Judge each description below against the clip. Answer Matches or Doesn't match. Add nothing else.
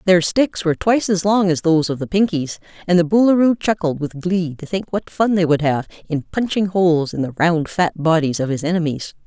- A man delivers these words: Doesn't match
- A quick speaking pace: Matches